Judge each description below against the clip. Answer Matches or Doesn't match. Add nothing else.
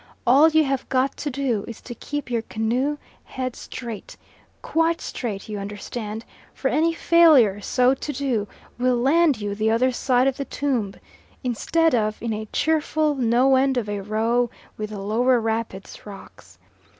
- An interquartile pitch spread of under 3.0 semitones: Doesn't match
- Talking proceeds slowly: Doesn't match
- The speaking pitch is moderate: Doesn't match